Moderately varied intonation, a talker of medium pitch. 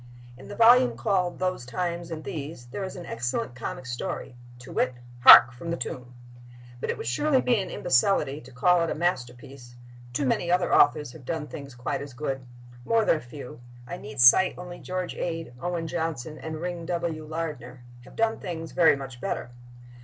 No: wide, 5.8 semitones; medium, 155 Hz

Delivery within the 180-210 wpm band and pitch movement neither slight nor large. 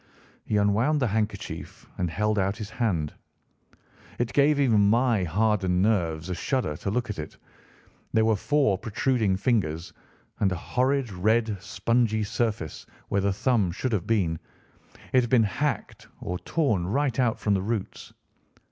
No: average, 155 wpm; average, 4.1 semitones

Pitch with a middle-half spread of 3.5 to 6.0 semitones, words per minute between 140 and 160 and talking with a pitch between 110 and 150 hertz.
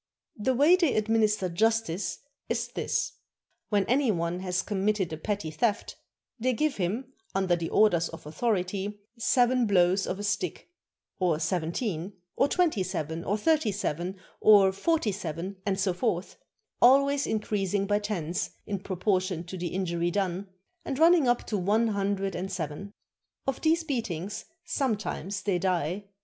No: average, 3.8 semitones; average, 155 wpm; high, 200 Hz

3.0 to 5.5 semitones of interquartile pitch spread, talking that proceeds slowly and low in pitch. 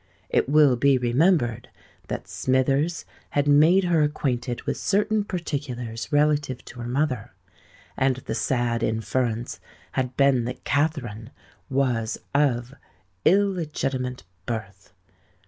Yes: average, 3.7 semitones; slow, 110 wpm; low, 130 Hz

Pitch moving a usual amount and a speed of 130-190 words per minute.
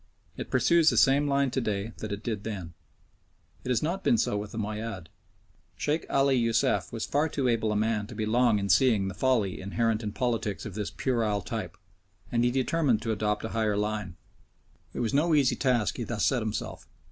No: average, 3.6 semitones; fast, 205 wpm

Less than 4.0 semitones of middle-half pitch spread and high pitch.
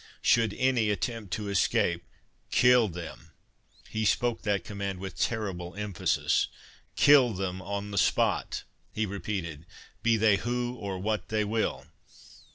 No: average, 2.9 semitones; low, 105 Hz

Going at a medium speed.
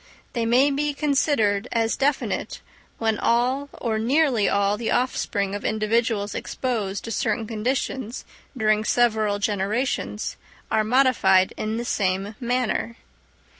No: slow, 125 wpm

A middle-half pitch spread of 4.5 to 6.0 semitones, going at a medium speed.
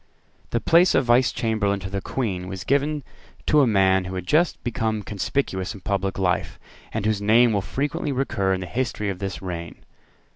Yes: average, 5.2 semitones; average, 190 wpm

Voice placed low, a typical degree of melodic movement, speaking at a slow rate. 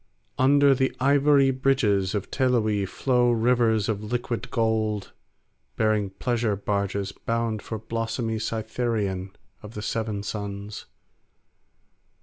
Yes: low, 110 Hz; average, 3.1 semitones; slow, 110 wpm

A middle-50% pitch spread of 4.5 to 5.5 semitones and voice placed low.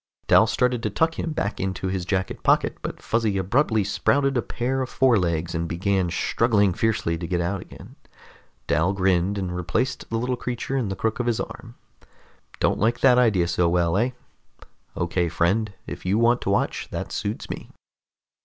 Yes: average, 4.9 semitones; low, 100 Hz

